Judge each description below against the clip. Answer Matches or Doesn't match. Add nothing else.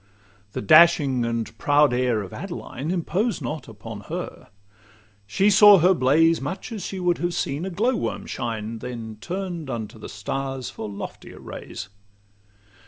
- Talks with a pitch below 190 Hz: Matches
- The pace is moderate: Matches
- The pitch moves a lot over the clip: Matches